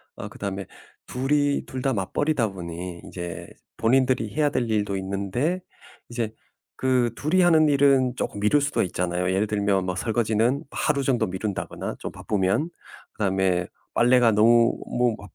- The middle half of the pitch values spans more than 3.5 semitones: Yes, wide, 5.4 semitones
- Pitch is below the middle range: Yes, low, 115 Hz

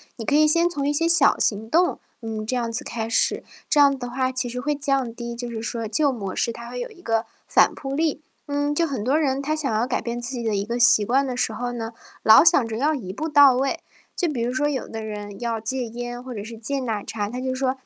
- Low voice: No, high, 245 Hz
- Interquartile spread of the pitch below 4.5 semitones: Yes, average, 3.7 semitones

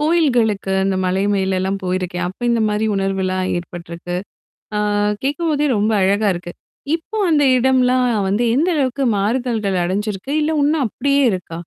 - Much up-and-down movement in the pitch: Yes, wide, 6.1 semitones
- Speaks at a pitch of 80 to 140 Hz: No, high, 210 Hz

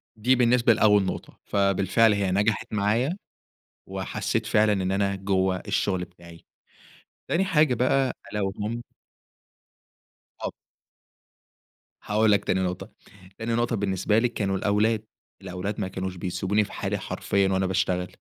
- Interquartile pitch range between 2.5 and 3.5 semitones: Yes, average, 2.9 semitones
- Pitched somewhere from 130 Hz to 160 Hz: No, low, 100 Hz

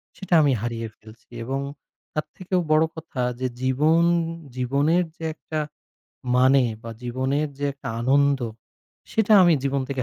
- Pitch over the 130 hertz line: Yes, medium, 140 Hz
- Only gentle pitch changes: No, average, 3.5 semitones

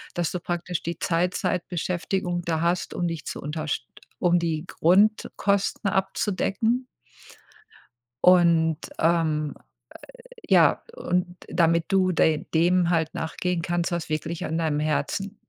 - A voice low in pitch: No, medium, 170 Hz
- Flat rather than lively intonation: Yes, narrow, 2.0 semitones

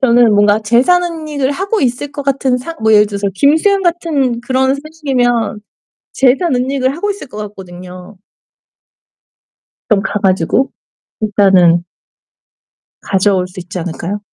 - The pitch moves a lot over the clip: Yes, wide, 5.8 semitones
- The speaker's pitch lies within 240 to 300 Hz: Yes, high, 245 Hz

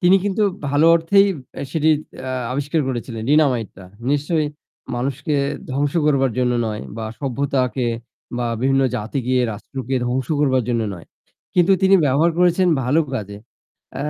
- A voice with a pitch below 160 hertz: Yes, low, 135 Hz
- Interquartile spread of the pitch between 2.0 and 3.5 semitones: No, average, 4.0 semitones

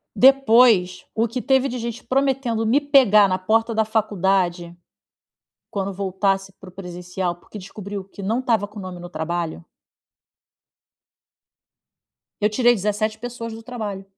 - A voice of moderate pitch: No, high, 210 Hz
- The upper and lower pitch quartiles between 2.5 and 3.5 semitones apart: No, average, 3.9 semitones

